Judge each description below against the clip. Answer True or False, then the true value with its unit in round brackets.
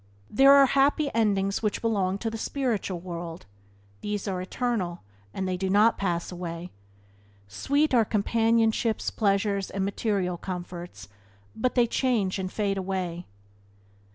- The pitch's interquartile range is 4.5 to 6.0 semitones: False (3.8 semitones)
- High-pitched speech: True (200 Hz)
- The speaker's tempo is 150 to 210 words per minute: False (135 wpm)